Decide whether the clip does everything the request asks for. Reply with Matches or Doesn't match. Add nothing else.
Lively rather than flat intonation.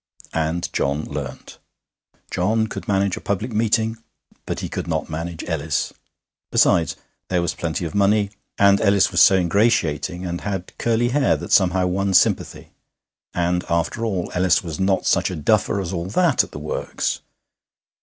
Doesn't match